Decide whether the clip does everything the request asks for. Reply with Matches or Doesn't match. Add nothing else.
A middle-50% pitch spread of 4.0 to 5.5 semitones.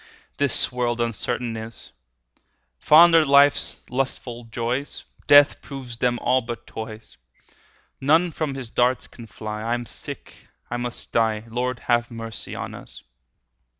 Doesn't match